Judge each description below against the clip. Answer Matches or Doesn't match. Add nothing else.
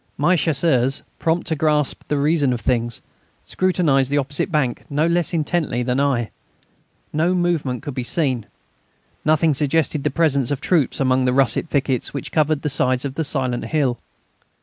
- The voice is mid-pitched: Matches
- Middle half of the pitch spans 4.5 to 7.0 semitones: Doesn't match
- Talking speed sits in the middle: Matches